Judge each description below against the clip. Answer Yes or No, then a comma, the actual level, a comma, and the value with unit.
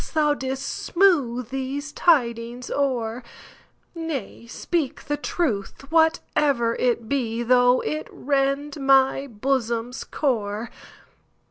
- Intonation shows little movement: No, average, 3.5 semitones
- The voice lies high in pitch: Yes, very high, 260 Hz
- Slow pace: Yes, slow, 90 wpm